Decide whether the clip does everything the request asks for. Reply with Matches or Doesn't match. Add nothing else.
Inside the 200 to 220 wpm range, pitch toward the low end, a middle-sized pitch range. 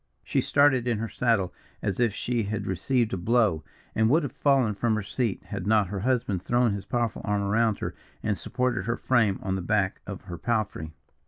Matches